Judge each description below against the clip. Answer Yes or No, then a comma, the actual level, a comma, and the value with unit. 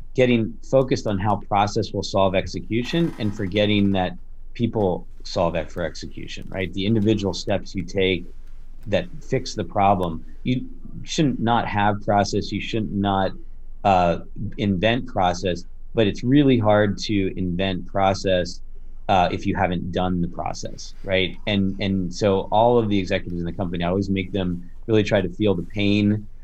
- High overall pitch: No, low, 100 Hz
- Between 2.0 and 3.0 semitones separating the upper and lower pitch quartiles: Yes, narrow, 2.5 semitones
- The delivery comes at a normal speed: Yes, average, 165 wpm